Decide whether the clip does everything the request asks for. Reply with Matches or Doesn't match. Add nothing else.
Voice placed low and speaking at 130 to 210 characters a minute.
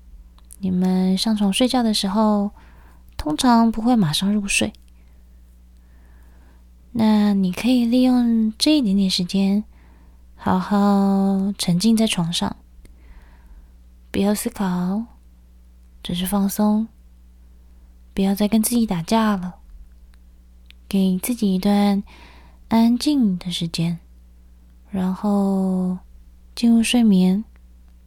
Doesn't match